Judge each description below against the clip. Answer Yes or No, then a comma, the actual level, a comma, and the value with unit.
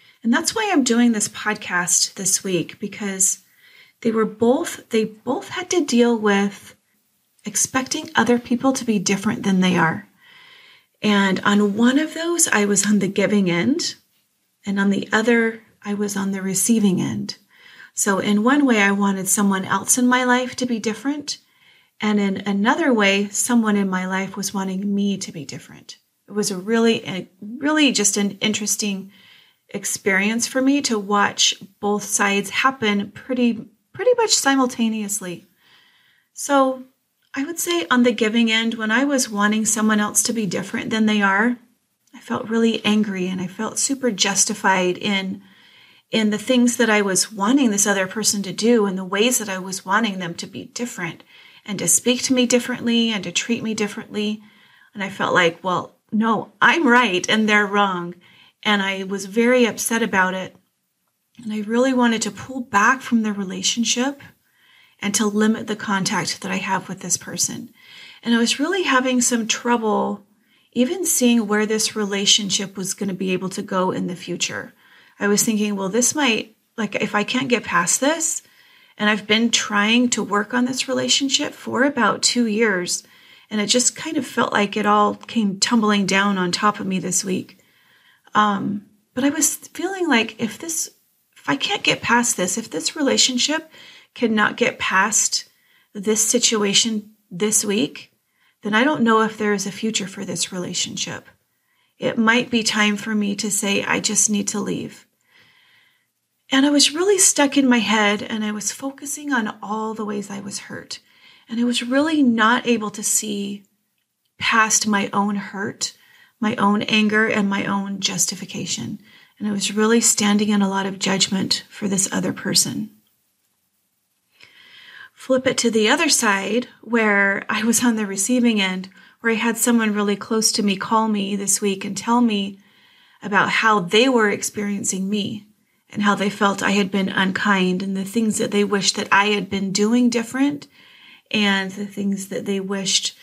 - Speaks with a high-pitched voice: Yes, high, 215 Hz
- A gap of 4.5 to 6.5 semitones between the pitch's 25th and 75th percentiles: No, average, 3.3 semitones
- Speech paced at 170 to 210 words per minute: Yes, average, 180 wpm